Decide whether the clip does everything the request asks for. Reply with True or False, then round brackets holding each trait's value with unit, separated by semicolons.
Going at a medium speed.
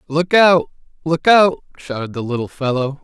True (160 wpm)